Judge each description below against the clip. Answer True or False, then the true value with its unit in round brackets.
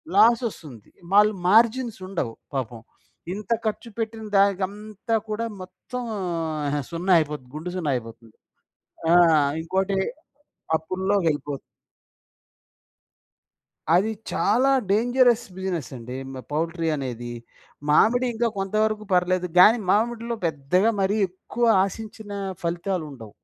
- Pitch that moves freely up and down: True (5.8 semitones)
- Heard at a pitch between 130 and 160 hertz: False (190 Hz)